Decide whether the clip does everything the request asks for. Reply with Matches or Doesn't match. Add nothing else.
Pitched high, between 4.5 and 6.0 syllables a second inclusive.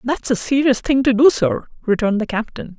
Matches